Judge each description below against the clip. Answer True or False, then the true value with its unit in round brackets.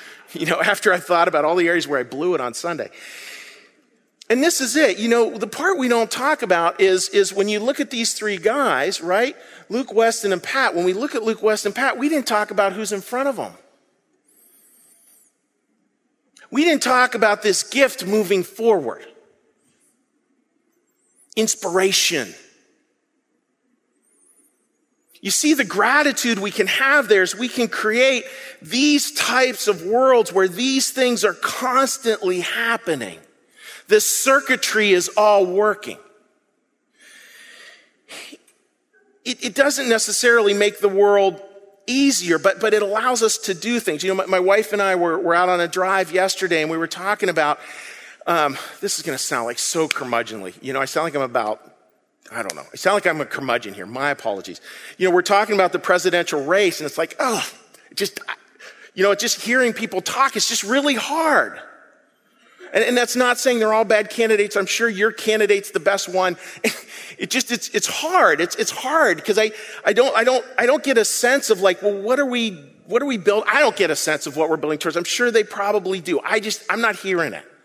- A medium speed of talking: True (190 wpm)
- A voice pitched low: False (215 Hz)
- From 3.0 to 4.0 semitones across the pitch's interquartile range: False (4.8 semitones)